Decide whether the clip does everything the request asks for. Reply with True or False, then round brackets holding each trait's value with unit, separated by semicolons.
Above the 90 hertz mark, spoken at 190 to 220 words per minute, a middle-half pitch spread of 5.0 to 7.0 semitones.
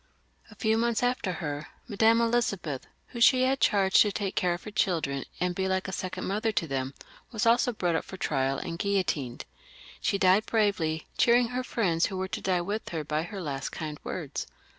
True (190 Hz; 205 wpm; 5.3 semitones)